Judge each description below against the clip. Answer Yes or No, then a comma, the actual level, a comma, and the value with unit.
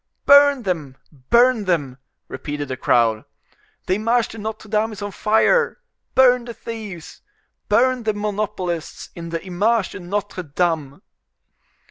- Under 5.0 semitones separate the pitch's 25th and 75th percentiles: No, average, 5.3 semitones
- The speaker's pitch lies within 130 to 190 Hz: No, high, 205 Hz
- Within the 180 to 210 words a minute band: No, slow, 135 wpm